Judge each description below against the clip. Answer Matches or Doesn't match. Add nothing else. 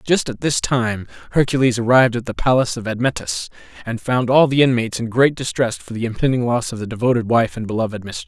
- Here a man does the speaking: Matches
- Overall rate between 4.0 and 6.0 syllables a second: Doesn't match